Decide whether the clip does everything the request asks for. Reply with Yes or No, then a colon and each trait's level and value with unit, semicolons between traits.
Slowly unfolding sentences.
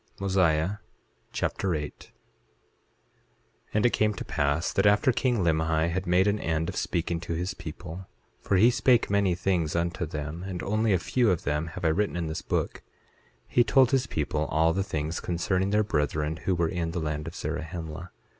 No: average, 190 wpm